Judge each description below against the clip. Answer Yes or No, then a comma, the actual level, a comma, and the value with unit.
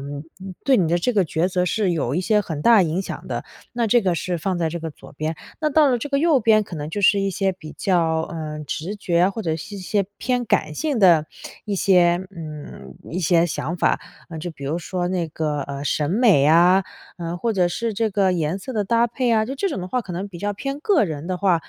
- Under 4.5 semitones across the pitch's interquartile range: No, average, 4.8 semitones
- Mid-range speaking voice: Yes, medium, 180 Hz